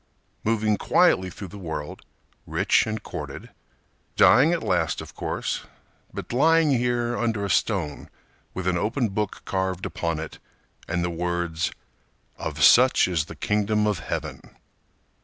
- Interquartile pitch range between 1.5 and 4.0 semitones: No, average, 4.7 semitones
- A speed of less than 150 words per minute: Yes, average, 140 wpm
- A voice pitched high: No, low, 100 Hz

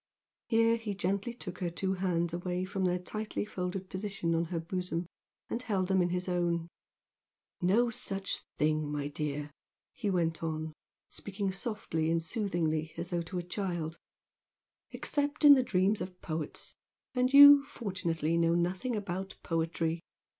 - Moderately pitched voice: Yes, medium, 180 Hz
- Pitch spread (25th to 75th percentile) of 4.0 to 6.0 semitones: No, average, 3.3 semitones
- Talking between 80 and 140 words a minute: No, average, 155 wpm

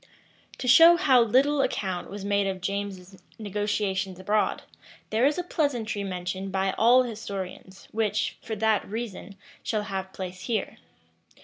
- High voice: Yes, high, 205 Hz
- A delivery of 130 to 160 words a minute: Yes, average, 140 wpm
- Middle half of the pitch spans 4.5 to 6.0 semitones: No, average, 3.3 semitones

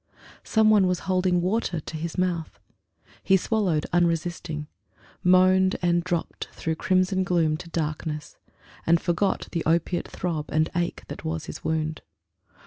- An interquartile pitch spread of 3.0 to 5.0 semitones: No, narrow, 2.5 semitones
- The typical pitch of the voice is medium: Yes, medium, 175 Hz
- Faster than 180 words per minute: No, average, 140 wpm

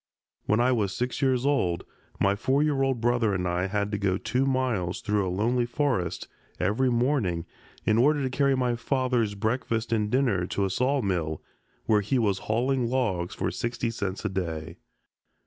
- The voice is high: No, low, 115 Hz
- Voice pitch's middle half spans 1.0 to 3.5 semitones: No, average, 4.8 semitones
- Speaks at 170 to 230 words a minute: Yes, average, 180 wpm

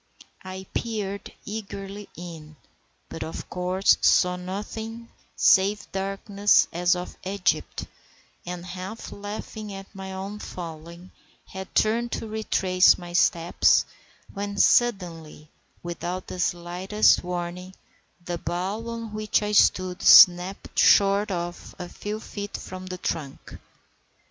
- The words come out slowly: Yes, slow, 120 wpm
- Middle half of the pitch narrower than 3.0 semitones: Yes, narrow, 2.6 semitones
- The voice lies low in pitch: No, high, 190 Hz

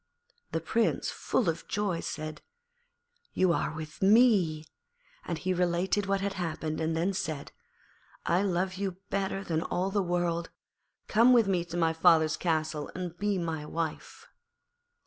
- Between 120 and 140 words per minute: No, average, 150 wpm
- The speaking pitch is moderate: Yes, medium, 175 Hz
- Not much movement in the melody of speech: No, average, 3.1 semitones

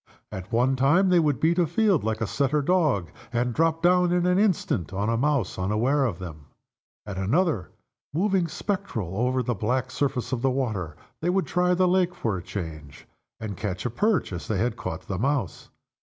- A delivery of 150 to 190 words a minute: No, average, 200 wpm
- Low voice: Yes, low, 130 Hz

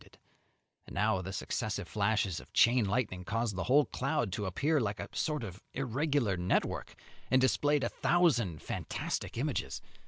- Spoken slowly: No, average, 155 wpm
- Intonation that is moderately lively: No, wide, 5.7 semitones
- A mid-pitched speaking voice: No, low, 110 Hz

